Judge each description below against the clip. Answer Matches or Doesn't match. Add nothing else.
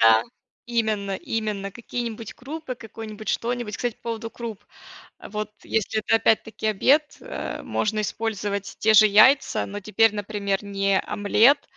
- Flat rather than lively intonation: Matches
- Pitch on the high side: Matches